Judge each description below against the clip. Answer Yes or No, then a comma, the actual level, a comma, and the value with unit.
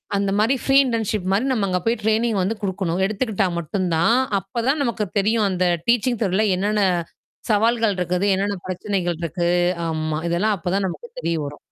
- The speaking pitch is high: Yes, high, 200 Hz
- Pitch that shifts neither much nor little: Yes, average, 3.5 semitones